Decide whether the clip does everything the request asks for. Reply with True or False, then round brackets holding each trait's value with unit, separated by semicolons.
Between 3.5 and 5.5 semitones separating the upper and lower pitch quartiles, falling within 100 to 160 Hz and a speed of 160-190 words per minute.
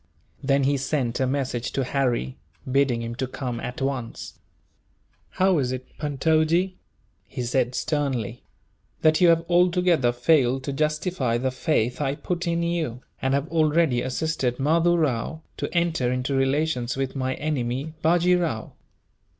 False (4.1 semitones; 140 Hz; 150 wpm)